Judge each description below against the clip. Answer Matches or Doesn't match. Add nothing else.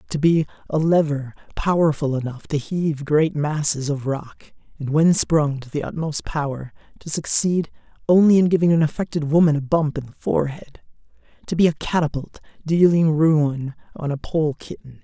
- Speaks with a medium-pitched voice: Matches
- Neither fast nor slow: Matches